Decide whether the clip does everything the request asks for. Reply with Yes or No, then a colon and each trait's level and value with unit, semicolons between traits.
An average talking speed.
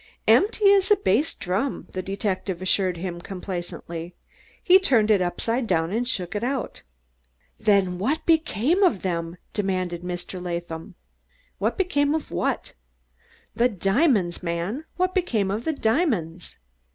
No: slow, 130 wpm